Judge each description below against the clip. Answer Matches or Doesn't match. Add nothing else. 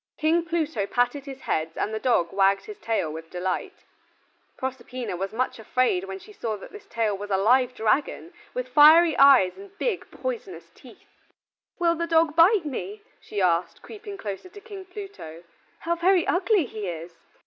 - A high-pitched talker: Matches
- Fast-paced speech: Doesn't match